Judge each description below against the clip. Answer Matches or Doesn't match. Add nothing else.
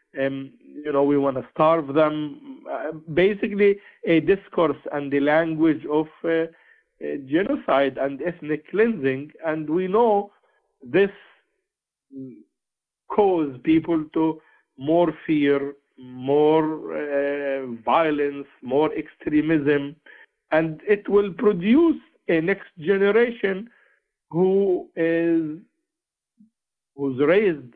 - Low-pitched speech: Doesn't match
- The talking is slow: Matches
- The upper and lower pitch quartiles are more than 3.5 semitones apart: Matches